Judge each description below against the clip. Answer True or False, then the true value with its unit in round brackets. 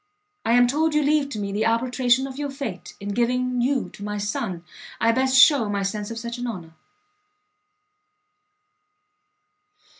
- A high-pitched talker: True (240 Hz)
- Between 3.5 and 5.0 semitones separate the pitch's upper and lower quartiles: True (4.1 semitones)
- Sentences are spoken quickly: False (160 wpm)